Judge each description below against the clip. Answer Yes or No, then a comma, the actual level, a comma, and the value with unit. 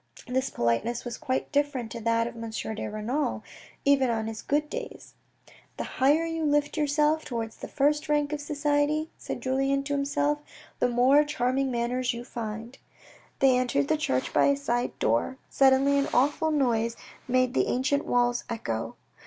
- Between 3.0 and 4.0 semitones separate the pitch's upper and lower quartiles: Yes, average, 3.5 semitones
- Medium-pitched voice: No, very high, 265 Hz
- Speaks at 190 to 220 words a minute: No, average, 170 wpm